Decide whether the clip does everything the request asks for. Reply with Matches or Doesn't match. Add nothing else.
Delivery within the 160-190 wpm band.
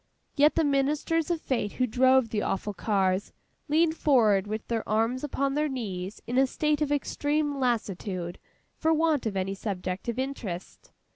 Matches